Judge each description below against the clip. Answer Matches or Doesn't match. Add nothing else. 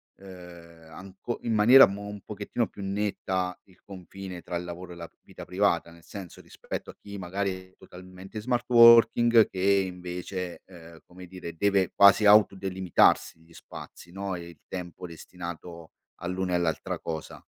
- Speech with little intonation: Matches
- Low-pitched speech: Matches